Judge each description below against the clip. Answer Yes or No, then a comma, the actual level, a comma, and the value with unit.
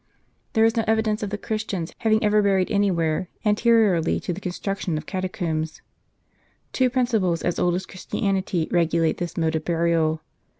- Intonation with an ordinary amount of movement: Yes, average, 4.1 semitones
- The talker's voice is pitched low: No, medium, 185 Hz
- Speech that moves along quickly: No, average, 165 wpm